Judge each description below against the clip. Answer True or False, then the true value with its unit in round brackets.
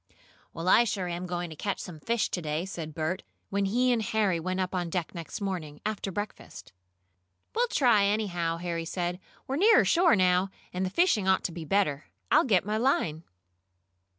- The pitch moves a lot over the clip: False (3.7 semitones)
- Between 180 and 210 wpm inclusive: True (190 wpm)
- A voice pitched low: False (185 Hz)